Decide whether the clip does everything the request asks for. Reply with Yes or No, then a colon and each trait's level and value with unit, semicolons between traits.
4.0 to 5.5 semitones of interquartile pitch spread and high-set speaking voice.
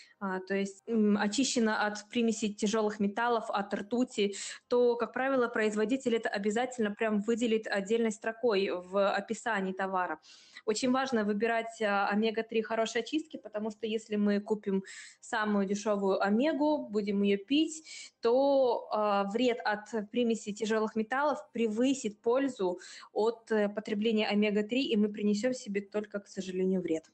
No: narrow, 2.5 semitones; high, 220 Hz